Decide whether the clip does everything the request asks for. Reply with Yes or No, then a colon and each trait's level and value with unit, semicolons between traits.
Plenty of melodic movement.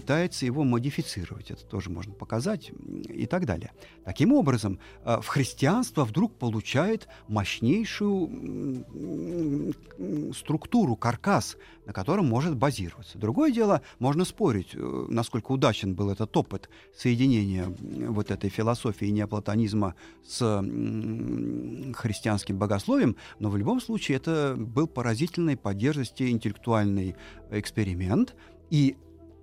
Yes: wide, 6.1 semitones